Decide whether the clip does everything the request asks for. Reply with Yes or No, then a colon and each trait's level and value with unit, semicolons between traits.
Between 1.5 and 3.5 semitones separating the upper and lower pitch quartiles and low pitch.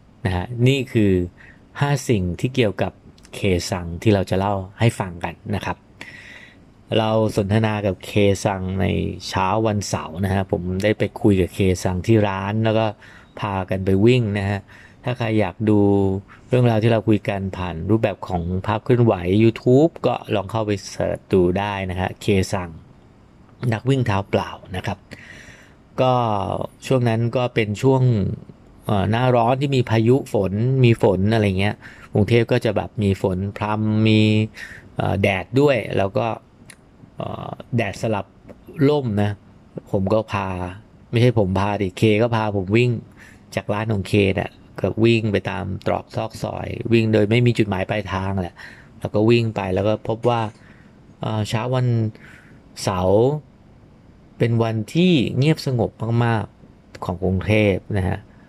Yes: average, 2.9 semitones; low, 105 Hz